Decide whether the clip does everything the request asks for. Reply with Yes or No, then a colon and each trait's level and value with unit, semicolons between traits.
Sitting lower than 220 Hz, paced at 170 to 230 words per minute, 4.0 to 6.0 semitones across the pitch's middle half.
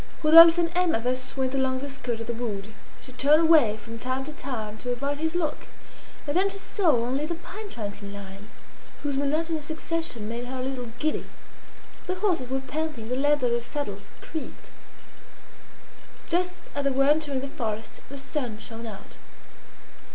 No: very high, 270 Hz; average, 180 wpm; average, 4.8 semitones